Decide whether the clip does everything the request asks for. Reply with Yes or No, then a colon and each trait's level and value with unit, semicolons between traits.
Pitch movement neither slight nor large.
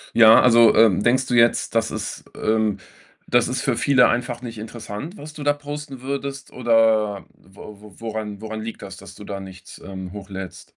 Yes: average, 3.5 semitones